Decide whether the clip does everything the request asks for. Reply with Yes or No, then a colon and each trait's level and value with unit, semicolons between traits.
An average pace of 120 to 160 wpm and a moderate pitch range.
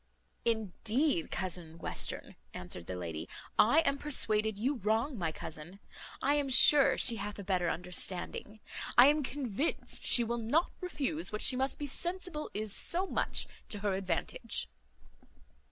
No: average, 150 wpm; wide, 7.3 semitones